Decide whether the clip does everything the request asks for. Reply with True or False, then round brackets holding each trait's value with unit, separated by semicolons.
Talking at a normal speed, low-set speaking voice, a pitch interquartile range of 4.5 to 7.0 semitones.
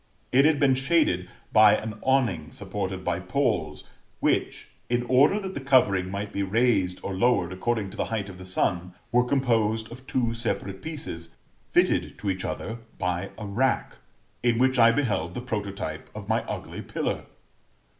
True (170 wpm; 110 Hz; 5.1 semitones)